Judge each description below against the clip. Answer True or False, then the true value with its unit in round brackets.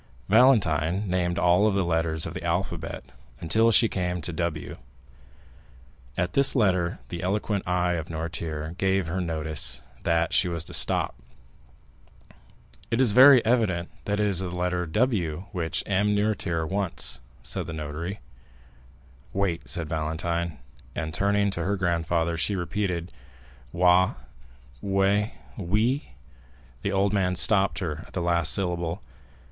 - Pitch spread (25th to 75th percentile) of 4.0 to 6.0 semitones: False (3.3 semitones)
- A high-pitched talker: False (90 Hz)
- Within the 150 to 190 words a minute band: False (135 wpm)